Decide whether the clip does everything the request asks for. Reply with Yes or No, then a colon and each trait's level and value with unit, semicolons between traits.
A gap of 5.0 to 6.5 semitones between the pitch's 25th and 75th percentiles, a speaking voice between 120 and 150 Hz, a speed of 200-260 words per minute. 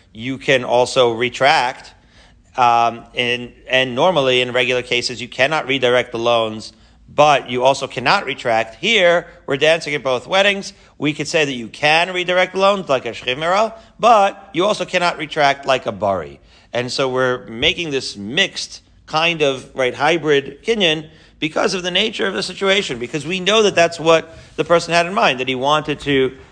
No: wide, 5.6 semitones; medium, 140 Hz; average, 180 wpm